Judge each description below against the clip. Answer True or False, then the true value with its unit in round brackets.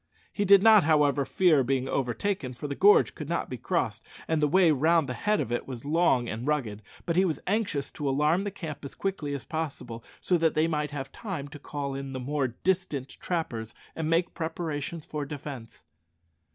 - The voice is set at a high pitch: False (150 Hz)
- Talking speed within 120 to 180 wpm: False (205 wpm)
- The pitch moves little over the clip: False (4.0 semitones)